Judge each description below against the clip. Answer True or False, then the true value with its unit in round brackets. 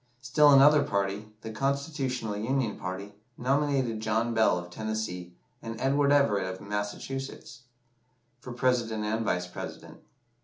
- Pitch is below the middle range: True (115 Hz)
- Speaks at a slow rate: True (125 wpm)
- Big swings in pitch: False (4.7 semitones)